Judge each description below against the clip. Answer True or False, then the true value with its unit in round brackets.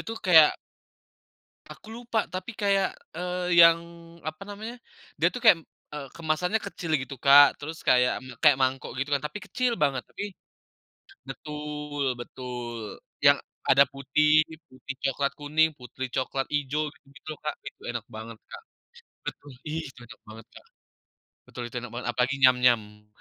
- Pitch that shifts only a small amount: False (4.3 semitones)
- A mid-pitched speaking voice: True (145 Hz)